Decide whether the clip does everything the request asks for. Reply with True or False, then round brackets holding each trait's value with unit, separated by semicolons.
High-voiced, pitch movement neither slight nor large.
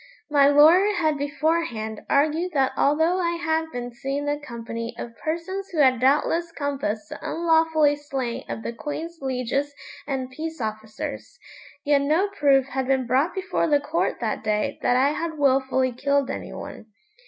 True (285 Hz; 3.9 semitones)